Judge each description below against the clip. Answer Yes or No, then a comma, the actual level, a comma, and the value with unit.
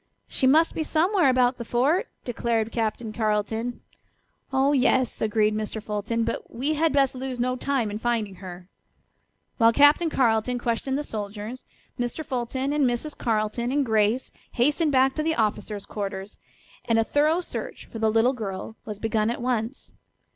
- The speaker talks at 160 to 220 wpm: Yes, average, 165 wpm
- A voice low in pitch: No, high, 240 Hz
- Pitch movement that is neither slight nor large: Yes, average, 3.7 semitones